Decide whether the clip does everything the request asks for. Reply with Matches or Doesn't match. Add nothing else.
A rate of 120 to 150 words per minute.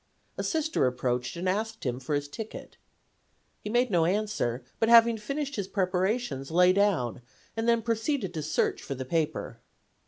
Doesn't match